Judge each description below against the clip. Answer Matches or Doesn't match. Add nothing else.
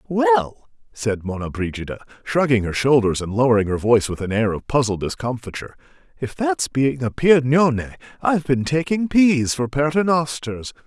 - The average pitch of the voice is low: Matches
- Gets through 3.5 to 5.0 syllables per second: Doesn't match